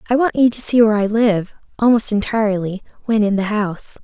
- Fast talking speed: Yes, fast, 210 wpm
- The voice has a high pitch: Yes, high, 215 Hz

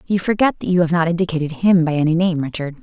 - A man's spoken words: No, female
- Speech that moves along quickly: Yes, fast, 255 wpm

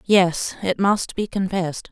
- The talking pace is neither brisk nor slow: Yes, average, 155 wpm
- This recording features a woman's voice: Yes, female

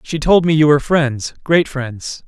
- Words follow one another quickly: No, average, 185 wpm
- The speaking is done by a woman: No, male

